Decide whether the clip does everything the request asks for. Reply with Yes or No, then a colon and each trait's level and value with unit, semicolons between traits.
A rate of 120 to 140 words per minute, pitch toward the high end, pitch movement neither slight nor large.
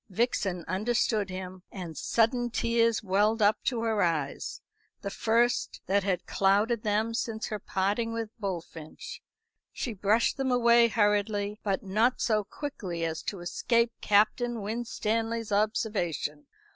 Yes: slow, 135 wpm; high, 215 Hz; average, 3.1 semitones